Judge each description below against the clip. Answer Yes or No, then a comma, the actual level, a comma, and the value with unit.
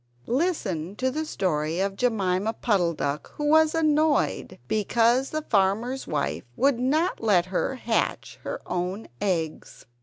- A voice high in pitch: Yes, high, 225 Hz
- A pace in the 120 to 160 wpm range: Yes, average, 140 wpm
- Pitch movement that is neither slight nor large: No, wide, 6.9 semitones